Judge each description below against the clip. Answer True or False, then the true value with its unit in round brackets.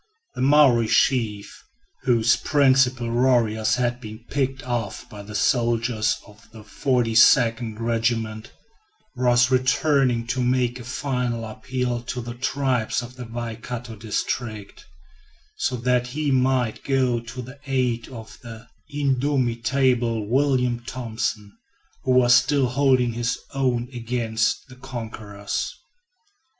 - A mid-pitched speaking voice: False (120 Hz)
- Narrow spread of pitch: True (2.0 semitones)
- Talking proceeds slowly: True (120 wpm)